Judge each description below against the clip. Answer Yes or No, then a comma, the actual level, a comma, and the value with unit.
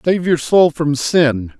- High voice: No, medium, 150 Hz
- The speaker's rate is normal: Yes, average, 190 wpm